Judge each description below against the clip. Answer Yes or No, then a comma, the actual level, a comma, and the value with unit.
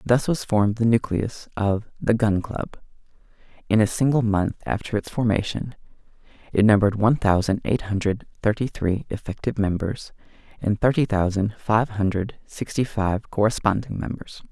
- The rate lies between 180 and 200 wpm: No, average, 145 wpm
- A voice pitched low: Yes, low, 105 Hz